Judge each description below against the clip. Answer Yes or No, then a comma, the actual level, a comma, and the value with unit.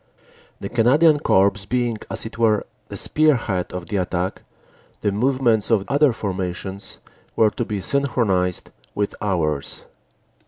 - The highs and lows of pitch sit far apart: No, average, 4.3 semitones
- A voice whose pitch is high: No, low, 105 Hz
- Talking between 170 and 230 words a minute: No, slow, 135 wpm